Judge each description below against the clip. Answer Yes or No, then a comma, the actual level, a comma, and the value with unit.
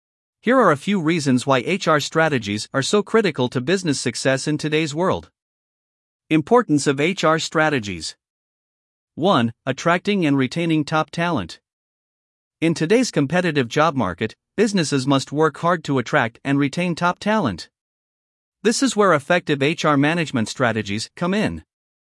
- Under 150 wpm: Yes, average, 140 wpm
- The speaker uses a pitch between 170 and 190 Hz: No, medium, 155 Hz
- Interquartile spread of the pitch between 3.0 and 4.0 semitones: No, average, 4.6 semitones